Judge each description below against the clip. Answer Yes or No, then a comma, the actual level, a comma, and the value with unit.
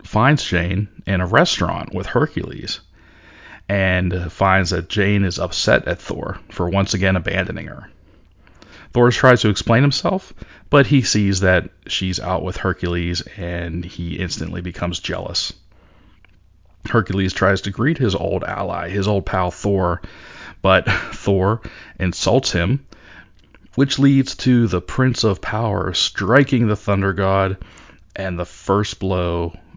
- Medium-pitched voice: No, very low, 95 Hz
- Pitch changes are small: No, average, 3.0 semitones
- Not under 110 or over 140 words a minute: Yes, slow, 135 wpm